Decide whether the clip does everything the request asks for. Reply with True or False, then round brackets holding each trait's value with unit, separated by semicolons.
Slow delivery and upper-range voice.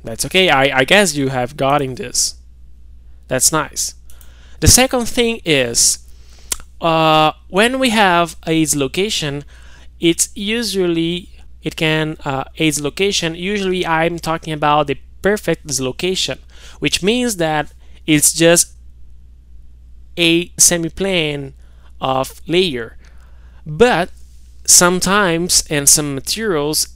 False (110 wpm; 150 Hz)